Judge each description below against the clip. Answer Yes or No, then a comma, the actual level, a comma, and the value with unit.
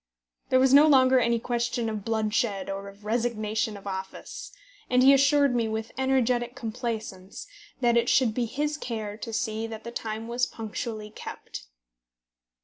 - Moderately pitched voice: No, high, 230 Hz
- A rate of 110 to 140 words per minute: No, average, 160 wpm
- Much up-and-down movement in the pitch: No, average, 2.7 semitones